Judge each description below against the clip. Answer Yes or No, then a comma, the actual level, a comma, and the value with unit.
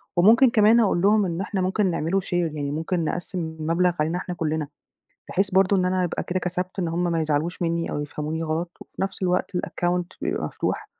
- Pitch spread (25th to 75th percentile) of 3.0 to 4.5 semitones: No, narrow, 2.5 semitones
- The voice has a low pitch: No, medium, 175 Hz